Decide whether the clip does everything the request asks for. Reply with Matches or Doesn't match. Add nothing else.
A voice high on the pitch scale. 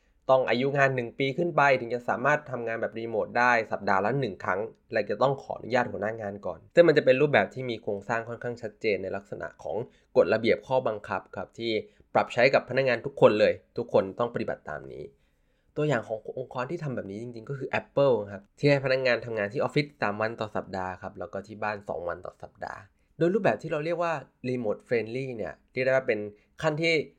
Doesn't match